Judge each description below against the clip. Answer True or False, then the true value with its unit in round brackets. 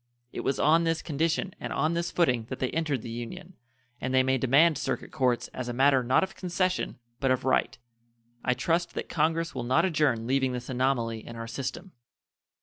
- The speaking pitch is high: False (135 Hz)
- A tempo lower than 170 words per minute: False (200 wpm)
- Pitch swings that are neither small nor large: True (4.7 semitones)